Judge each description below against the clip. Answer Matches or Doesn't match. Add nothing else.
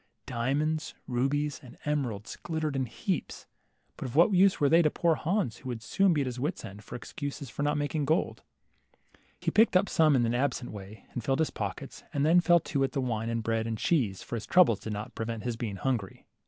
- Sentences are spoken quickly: Matches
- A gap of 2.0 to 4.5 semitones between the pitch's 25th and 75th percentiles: Doesn't match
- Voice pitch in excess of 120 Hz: Matches